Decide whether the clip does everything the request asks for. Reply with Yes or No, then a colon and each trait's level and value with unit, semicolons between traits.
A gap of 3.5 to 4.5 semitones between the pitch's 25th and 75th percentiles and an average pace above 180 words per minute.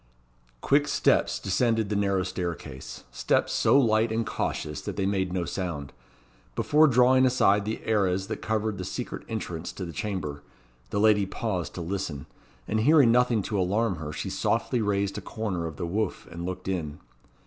No: average, 3.9 semitones; average, 175 wpm